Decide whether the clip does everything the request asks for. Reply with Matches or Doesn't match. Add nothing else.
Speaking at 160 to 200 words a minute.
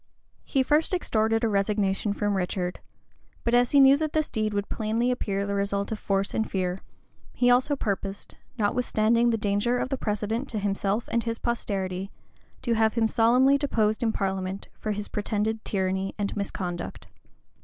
Matches